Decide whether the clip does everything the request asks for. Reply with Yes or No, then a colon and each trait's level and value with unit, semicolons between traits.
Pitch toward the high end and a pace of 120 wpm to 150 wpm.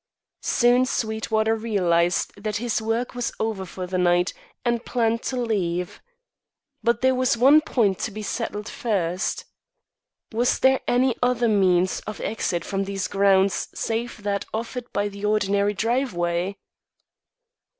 Yes: high, 215 Hz; average, 140 wpm